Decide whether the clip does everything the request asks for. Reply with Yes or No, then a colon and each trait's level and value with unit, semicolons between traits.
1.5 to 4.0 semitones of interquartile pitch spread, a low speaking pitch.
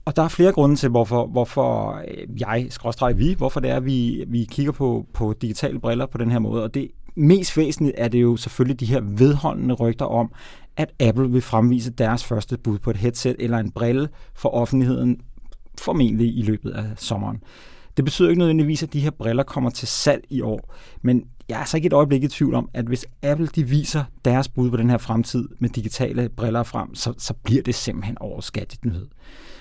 Yes: average, 3.0 semitones; low, 125 Hz